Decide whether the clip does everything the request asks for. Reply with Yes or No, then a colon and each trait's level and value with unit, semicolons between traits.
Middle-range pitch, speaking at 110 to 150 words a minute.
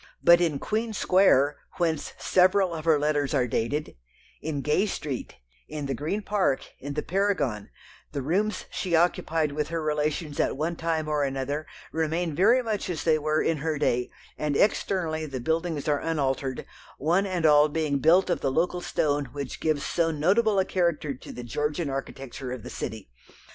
No: medium, 155 Hz; average, 180 wpm